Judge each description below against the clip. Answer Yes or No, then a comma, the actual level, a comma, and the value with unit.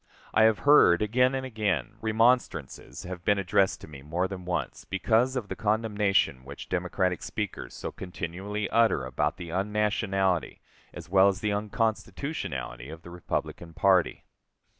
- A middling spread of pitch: Yes, average, 3.7 semitones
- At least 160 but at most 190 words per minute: No, average, 150 wpm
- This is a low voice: Yes, very low, 95 Hz